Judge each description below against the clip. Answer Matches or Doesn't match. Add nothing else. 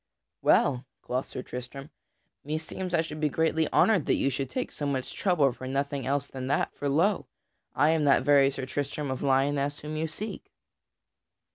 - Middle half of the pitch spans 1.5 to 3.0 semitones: Matches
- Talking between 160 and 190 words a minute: Matches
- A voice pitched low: Doesn't match